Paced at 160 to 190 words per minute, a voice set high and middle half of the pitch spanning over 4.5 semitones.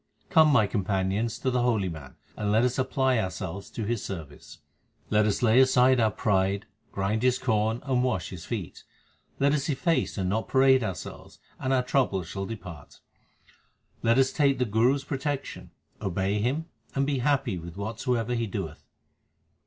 No: average, 170 wpm; low, 115 Hz; average, 5.0 semitones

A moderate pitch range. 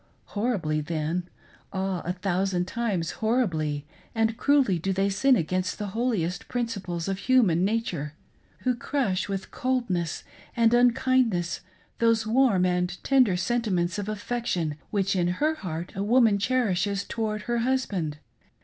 Yes: average, 5.0 semitones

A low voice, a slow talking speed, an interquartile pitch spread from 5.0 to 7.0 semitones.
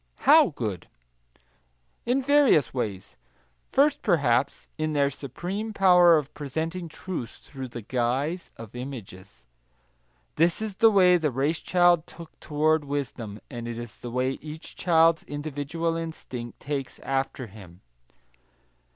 No: medium, 145 Hz; slow, 130 wpm; wide, 5.4 semitones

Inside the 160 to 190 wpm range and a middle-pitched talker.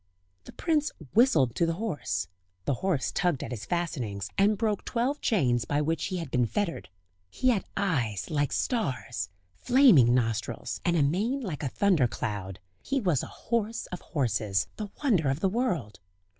Yes: average, 170 wpm; medium, 165 Hz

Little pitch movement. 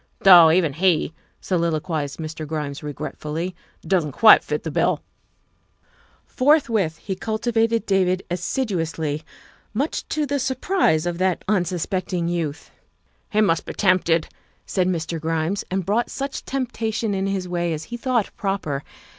No: average, 5.0 semitones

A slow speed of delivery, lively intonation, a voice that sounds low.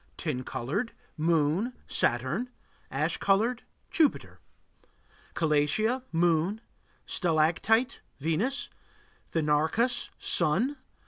No: slow, 70 wpm; wide, 7.1 semitones; medium, 170 Hz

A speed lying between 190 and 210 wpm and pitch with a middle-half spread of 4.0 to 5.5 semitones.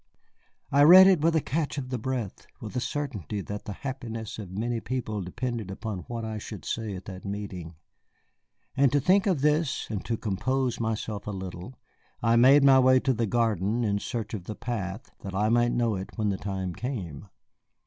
Yes: average, 200 wpm; average, 4.4 semitones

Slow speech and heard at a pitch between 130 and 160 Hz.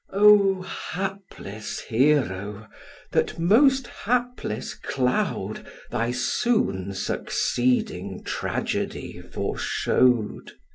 Yes: slow, 65 wpm; medium, 140 Hz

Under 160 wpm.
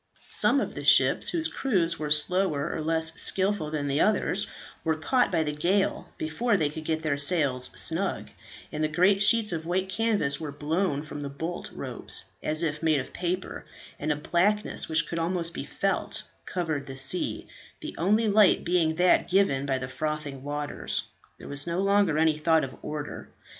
No: average, 185 wpm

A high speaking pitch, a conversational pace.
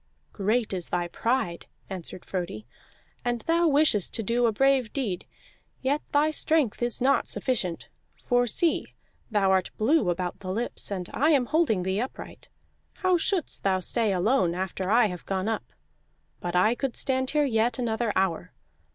Yes: high, 225 Hz; average, 165 wpm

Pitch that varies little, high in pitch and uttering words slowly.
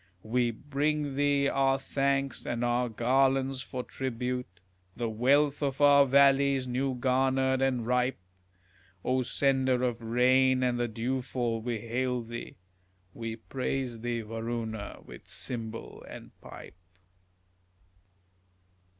No: narrow, 2.2 semitones; low, 125 Hz; slow, 115 wpm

